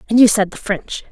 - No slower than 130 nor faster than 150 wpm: No, fast, 270 wpm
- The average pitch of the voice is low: No, high, 210 Hz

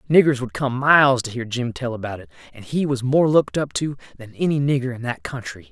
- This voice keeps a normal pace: No, fast, 240 wpm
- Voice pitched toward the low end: Yes, low, 130 Hz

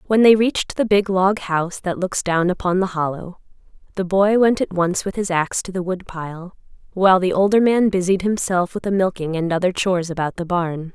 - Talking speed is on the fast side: Yes, fast, 215 wpm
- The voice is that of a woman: Yes, female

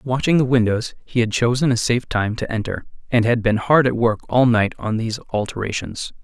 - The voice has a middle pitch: No, low, 115 Hz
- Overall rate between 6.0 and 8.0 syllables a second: No, 5.5 syllables/s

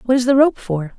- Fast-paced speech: Yes, fast, 305 wpm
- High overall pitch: Yes, high, 240 Hz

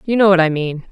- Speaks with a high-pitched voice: No, medium, 180 Hz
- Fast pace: Yes, fast, 330 wpm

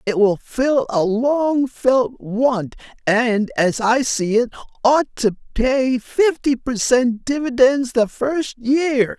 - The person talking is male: Yes, male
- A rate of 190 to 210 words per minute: No, slow, 135 wpm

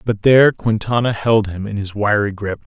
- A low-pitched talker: Yes, low, 105 Hz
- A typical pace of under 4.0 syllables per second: No, 5.1 syllables/s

